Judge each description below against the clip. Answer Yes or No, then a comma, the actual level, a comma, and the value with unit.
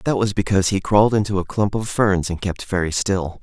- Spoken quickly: Yes, fast, 245 wpm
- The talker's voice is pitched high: No, low, 100 Hz